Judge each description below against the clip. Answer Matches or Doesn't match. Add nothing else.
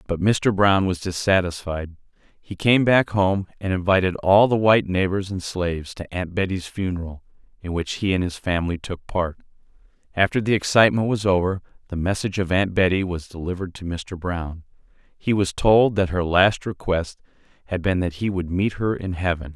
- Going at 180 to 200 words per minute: Matches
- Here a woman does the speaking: Doesn't match